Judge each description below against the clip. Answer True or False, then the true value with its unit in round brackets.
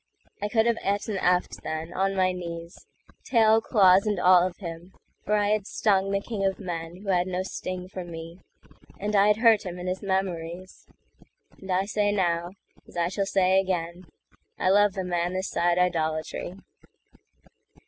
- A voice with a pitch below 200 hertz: True (185 Hz)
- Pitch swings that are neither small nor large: False (2.3 semitones)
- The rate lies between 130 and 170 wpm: True (165 wpm)